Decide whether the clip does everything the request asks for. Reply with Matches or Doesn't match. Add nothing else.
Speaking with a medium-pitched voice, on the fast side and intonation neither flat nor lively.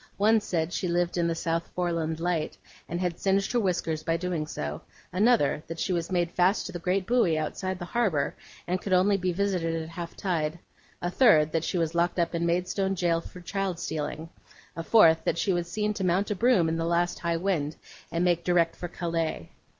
Doesn't match